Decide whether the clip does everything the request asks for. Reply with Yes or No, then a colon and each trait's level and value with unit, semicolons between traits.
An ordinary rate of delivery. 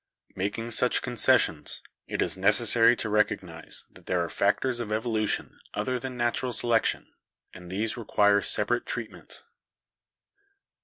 No: slow, 125 wpm